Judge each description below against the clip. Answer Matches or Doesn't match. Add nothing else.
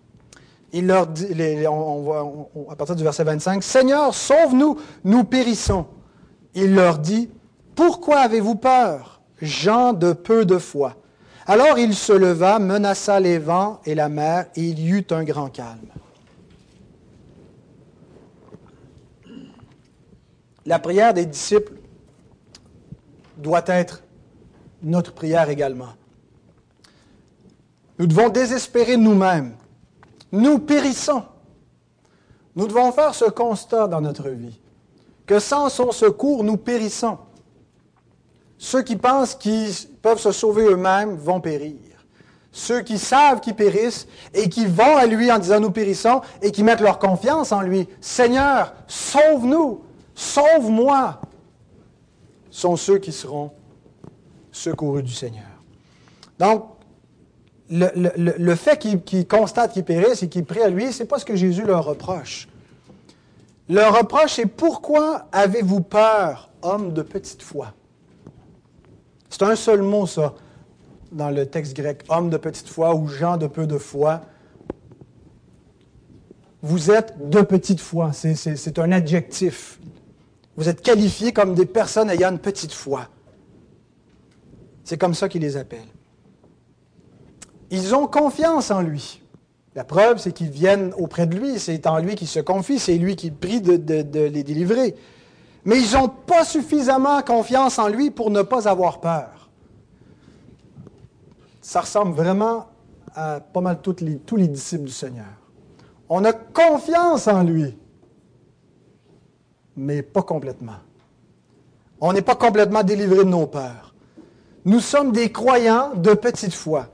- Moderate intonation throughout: Doesn't match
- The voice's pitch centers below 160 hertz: Doesn't match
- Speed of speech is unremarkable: Doesn't match